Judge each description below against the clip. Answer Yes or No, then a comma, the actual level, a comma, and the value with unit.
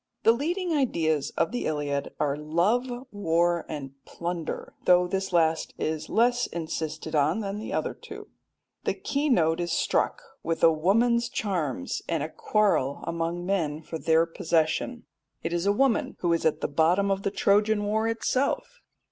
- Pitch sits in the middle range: Yes, medium, 175 Hz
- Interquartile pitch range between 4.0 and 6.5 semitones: Yes, average, 5.2 semitones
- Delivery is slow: No, average, 165 wpm